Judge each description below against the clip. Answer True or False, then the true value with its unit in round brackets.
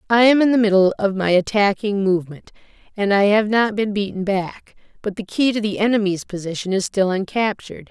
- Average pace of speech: True (195 wpm)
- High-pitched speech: True (200 Hz)